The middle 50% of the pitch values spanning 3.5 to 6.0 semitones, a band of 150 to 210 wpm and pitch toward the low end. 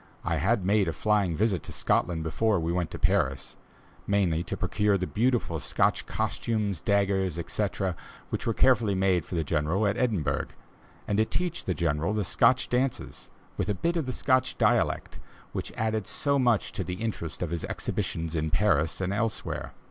Yes: average, 4.6 semitones; average, 180 wpm; low, 100 Hz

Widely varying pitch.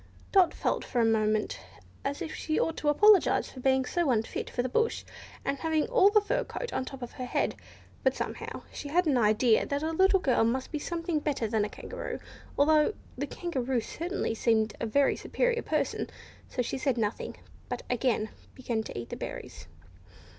Yes: wide, 5.9 semitones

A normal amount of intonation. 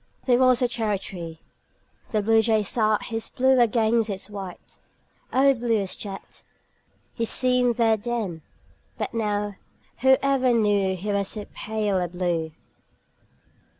Yes: average, 3.3 semitones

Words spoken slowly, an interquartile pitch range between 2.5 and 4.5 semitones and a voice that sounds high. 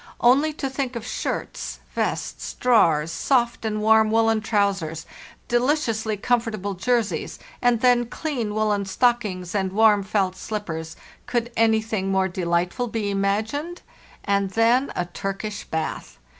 Yes: slow, 130 wpm; average, 3.5 semitones; high, 215 Hz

